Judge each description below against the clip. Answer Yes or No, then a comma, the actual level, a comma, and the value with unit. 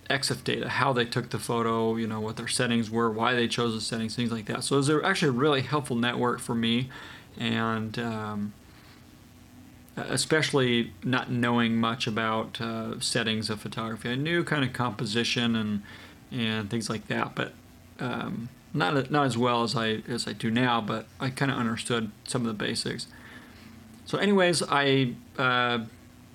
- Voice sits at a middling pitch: No, low, 120 Hz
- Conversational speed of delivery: Yes, average, 175 wpm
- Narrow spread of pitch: Yes, narrow, 2.1 semitones